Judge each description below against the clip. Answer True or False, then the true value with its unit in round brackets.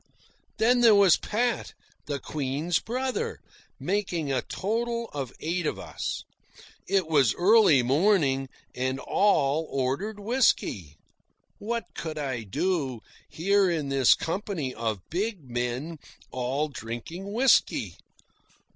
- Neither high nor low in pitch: True (160 Hz)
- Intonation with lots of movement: True (7.5 semitones)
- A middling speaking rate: False (115 wpm)